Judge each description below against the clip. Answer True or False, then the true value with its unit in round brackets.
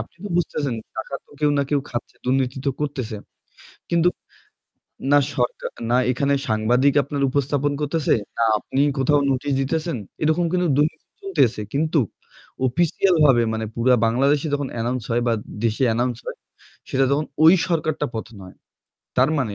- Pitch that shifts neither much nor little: True (3.6 semitones)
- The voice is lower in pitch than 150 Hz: True (140 Hz)